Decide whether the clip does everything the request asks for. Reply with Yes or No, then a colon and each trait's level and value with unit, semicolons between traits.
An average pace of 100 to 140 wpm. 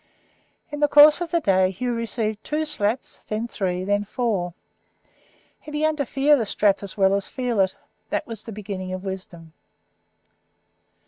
No: average, 175 wpm